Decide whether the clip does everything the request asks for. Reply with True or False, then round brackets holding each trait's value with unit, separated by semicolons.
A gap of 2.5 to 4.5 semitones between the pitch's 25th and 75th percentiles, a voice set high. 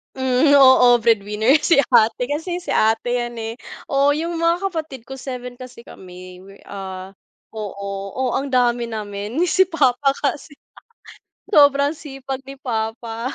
True (4.1 semitones; 250 Hz)